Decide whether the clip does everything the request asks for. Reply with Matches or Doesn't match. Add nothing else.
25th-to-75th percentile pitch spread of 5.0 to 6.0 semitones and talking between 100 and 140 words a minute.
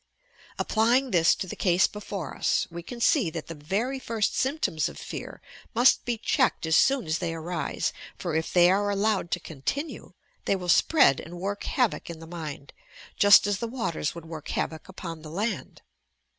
Doesn't match